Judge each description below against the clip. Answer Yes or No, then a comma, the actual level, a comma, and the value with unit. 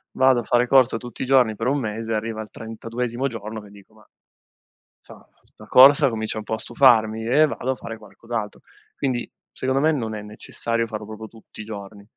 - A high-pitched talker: No, low, 115 Hz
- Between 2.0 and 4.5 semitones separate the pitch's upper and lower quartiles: Yes, narrow, 2.6 semitones